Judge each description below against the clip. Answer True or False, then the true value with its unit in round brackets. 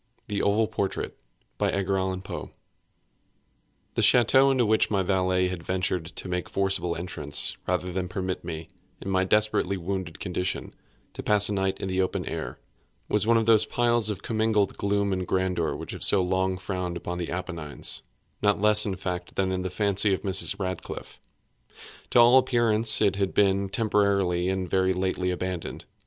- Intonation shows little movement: True (2.1 semitones)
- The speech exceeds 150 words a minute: True (165 wpm)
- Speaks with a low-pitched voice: True (95 Hz)